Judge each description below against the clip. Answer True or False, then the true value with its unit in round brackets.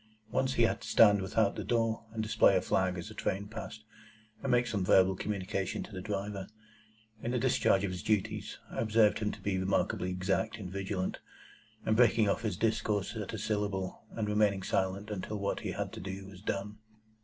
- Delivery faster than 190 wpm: True (200 wpm)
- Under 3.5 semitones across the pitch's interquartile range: True (2.4 semitones)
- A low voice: True (100 Hz)